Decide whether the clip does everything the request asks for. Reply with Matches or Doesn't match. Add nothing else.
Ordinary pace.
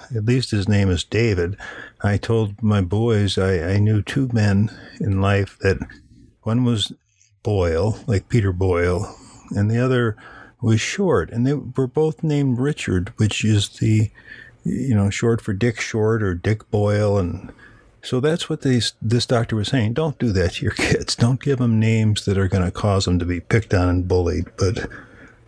Matches